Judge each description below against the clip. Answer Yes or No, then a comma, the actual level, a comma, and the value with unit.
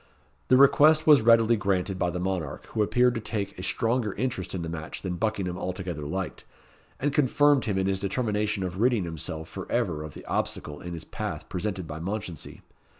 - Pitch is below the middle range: Yes, very low, 95 Hz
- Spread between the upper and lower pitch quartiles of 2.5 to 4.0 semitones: No, average, 4.6 semitones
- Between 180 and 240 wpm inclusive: Yes, average, 195 wpm